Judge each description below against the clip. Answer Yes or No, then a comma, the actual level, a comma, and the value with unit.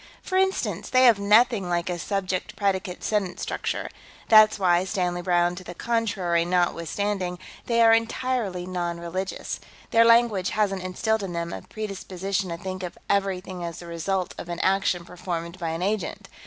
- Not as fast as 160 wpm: No, average, 170 wpm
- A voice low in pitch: No, medium, 185 Hz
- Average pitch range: Yes, average, 3.0 semitones